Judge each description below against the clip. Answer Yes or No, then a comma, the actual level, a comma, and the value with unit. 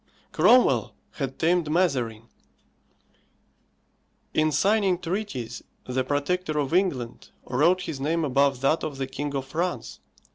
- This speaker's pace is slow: Yes, slow, 120 wpm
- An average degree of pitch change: Yes, average, 4.9 semitones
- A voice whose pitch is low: No, medium, 150 Hz